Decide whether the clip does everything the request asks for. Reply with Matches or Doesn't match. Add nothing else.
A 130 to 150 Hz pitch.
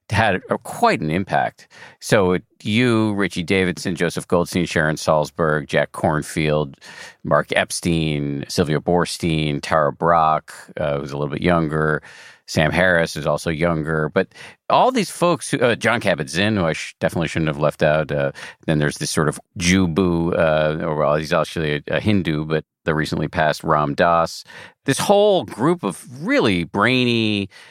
Doesn't match